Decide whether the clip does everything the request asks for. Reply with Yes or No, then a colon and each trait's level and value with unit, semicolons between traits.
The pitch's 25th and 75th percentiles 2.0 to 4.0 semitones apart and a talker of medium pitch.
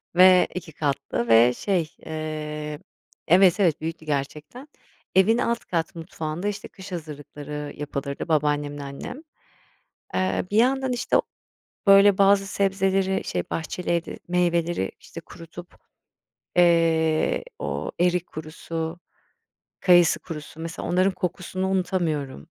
Yes: average, 3.6 semitones; medium, 170 Hz